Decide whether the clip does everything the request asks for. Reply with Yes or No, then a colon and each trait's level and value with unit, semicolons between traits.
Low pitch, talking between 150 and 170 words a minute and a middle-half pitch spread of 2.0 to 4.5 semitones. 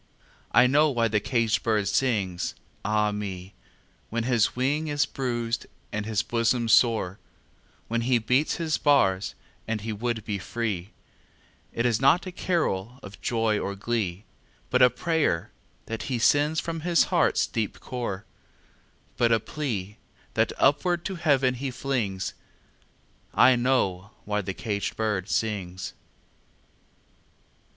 No: low, 115 Hz; average, 140 wpm; average, 4.2 semitones